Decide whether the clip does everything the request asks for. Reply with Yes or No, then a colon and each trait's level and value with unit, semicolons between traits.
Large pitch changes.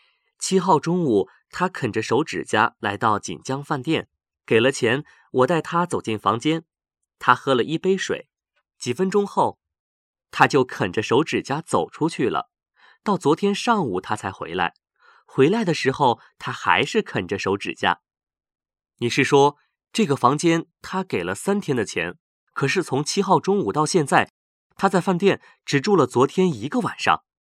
Yes: wide, 6.2 semitones